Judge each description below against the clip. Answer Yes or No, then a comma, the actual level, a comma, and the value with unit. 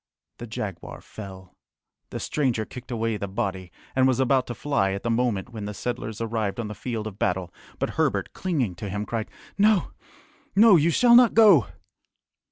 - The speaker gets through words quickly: No, average, 180 wpm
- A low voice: Yes, low, 115 Hz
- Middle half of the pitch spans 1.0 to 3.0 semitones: No, average, 4.7 semitones